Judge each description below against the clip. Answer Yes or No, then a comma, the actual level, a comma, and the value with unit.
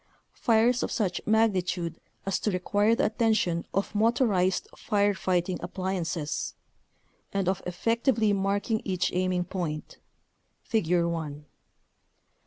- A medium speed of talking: No, slow, 115 wpm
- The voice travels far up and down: No, average, 3.5 semitones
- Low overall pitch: No, high, 190 Hz